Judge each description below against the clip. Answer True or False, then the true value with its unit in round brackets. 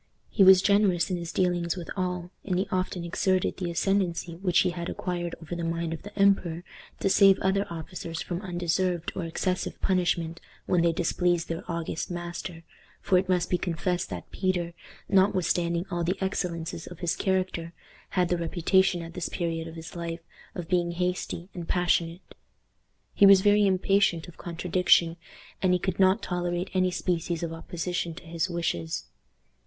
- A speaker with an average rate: True (170 wpm)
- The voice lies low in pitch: False (175 Hz)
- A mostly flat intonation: True (1.7 semitones)